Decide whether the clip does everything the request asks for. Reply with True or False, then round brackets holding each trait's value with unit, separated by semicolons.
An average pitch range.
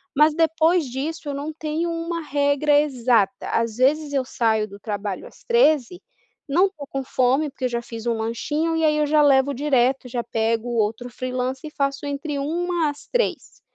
True (4.1 semitones)